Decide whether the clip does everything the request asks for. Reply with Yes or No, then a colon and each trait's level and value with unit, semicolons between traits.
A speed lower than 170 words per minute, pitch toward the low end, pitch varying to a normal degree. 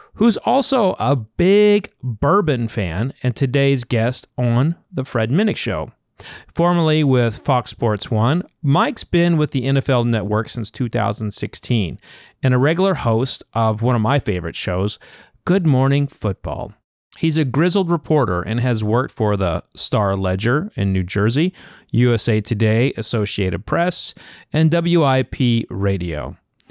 No: slow, 135 wpm; low, 125 Hz; wide, 6.1 semitones